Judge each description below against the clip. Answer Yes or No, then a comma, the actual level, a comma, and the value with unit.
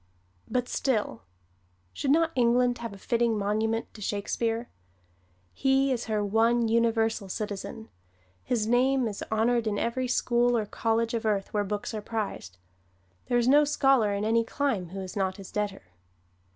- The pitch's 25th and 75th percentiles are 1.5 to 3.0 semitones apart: Yes, average, 2.7 semitones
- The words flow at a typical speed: Yes, average, 160 wpm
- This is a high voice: Yes, high, 225 Hz